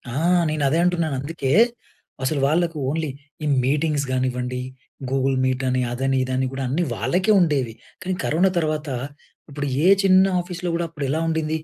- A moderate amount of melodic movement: Yes, average, 3.9 semitones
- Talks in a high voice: No, medium, 150 Hz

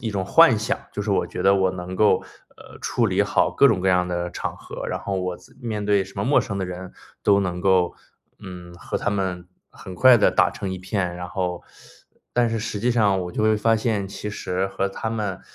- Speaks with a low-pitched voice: Yes, very low, 95 Hz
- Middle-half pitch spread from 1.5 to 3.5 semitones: Yes, average, 2.8 semitones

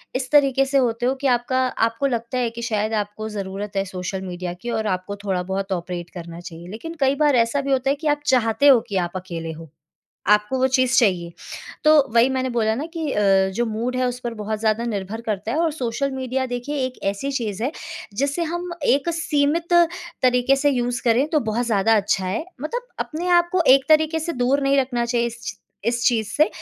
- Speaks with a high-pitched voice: Yes, high, 240 Hz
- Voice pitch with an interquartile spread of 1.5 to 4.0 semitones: No, average, 4.8 semitones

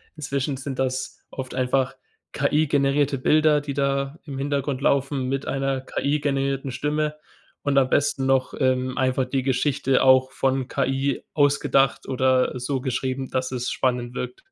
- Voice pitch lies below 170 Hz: Yes, low, 135 Hz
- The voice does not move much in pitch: Yes, narrow, 1.4 semitones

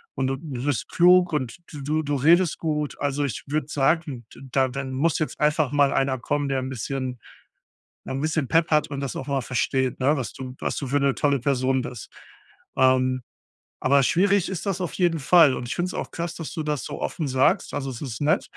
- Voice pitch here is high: No, medium, 140 Hz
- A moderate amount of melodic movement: Yes, average, 3.0 semitones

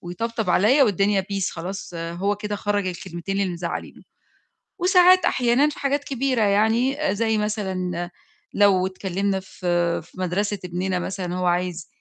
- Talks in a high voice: Yes, high, 195 Hz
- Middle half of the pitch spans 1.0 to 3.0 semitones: No, average, 3.6 semitones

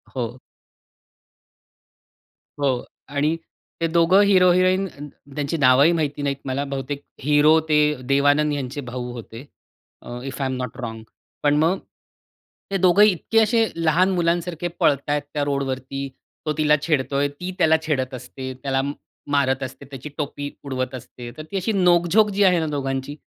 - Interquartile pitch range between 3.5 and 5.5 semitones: Yes, average, 4.1 semitones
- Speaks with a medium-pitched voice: Yes, medium, 145 Hz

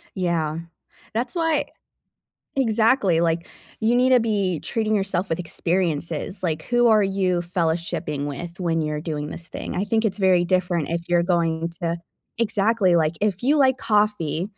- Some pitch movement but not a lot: Yes, average, 4.4 semitones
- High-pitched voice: No, medium, 180 Hz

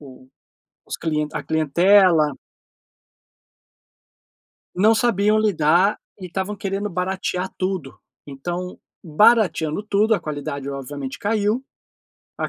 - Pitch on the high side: No, medium, 180 Hz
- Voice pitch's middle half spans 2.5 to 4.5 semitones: No, average, 5.2 semitones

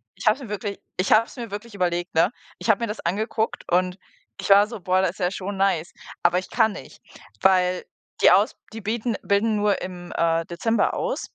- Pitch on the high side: Yes, high, 195 Hz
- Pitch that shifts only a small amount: No, average, 3.1 semitones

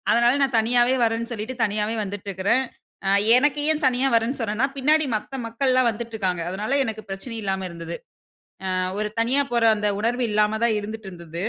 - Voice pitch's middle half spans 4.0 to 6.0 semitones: No, average, 3.2 semitones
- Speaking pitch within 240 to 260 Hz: No, high, 225 Hz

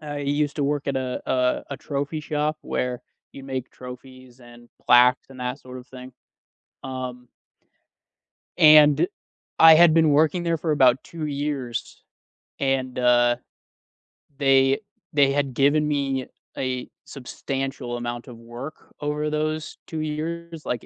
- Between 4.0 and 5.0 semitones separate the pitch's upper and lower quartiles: No, average, 3.0 semitones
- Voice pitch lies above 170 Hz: No, low, 135 Hz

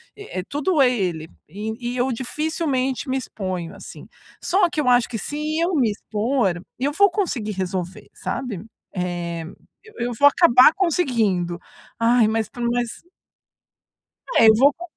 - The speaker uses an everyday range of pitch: No, wide, 6.1 semitones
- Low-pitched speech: No, high, 245 Hz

